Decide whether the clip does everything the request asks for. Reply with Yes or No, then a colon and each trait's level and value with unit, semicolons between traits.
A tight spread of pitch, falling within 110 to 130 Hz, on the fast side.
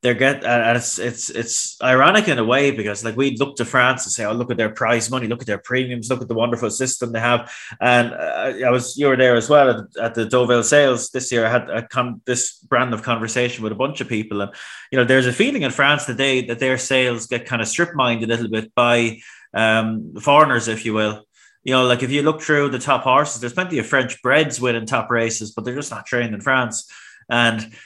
Yes: narrow, 2.2 semitones; low, 120 Hz; fast, 250 wpm